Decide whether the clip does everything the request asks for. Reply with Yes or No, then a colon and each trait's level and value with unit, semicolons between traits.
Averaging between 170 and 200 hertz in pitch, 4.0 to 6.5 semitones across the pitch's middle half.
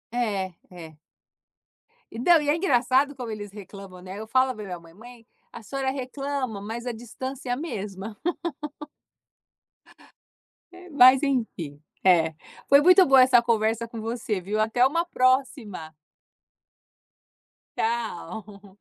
No: high, 230 Hz; average, 4.6 semitones